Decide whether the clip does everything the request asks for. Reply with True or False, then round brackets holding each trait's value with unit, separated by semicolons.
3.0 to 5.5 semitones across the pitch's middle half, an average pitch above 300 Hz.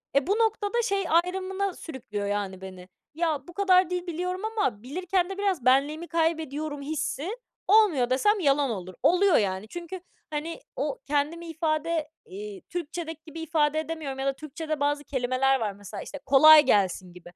True (5.1 semitones; 310 Hz)